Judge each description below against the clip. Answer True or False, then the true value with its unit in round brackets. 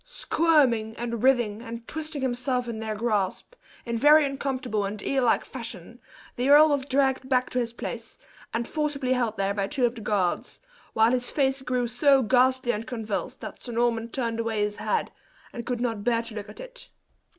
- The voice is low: False (240 Hz)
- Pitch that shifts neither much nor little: True (3.0 semitones)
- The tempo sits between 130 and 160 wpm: False (195 wpm)